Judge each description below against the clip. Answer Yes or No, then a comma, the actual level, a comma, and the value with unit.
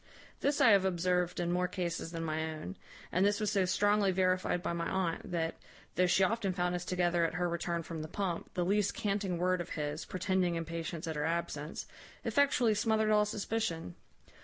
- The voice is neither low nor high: Yes, medium, 180 Hz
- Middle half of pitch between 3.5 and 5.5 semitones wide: No, average, 2.9 semitones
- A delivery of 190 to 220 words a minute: Yes, average, 195 wpm